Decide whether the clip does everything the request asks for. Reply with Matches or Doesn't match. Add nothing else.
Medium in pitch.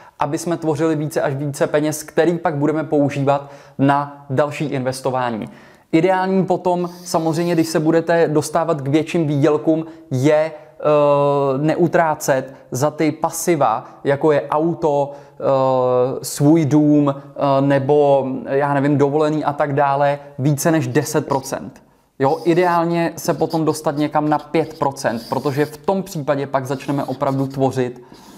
Matches